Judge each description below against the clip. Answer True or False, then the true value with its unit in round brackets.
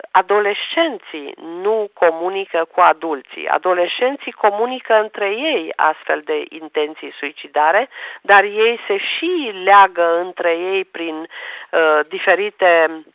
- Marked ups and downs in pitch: False (4.8 semitones)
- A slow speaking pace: True (105 wpm)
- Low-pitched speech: False (195 Hz)